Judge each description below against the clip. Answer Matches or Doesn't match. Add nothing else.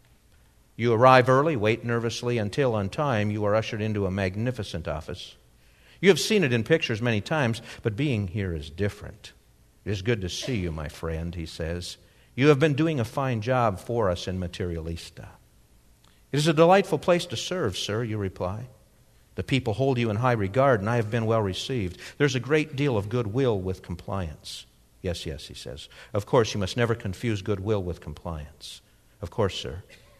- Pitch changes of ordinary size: Doesn't match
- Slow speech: Doesn't match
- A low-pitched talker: Matches